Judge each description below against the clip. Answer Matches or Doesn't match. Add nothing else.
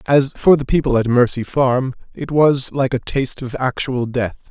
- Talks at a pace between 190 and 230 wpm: Matches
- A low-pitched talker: Matches